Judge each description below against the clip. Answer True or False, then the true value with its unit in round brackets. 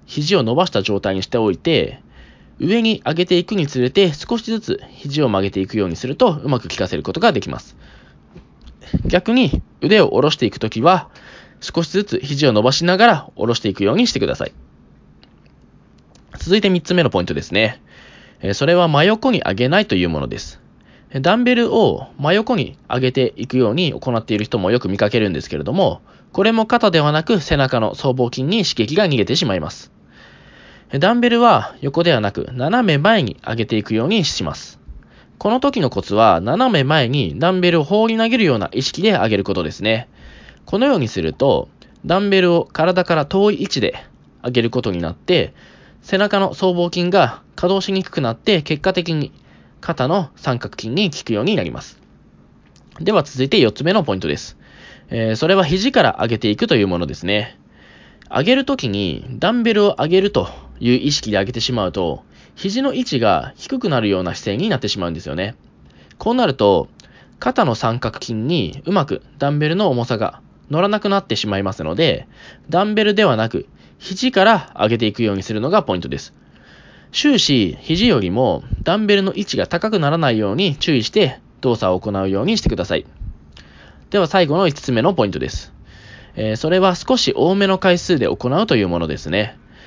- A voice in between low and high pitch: True (145 Hz)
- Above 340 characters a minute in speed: True (360 characters per minute)